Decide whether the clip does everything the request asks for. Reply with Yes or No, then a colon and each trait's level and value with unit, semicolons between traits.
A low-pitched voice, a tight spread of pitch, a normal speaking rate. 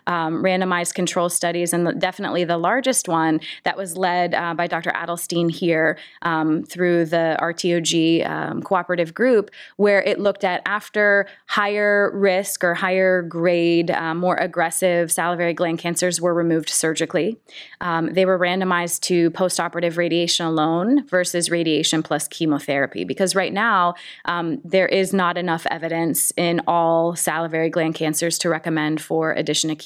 No: medium, 170 Hz; narrow, 1.8 semitones; average, 150 wpm